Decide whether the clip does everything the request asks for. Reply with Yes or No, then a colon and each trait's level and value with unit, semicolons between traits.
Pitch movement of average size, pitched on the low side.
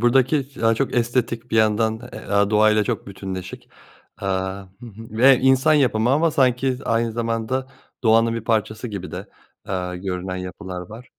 Yes: average, 3.8 semitones; low, 115 Hz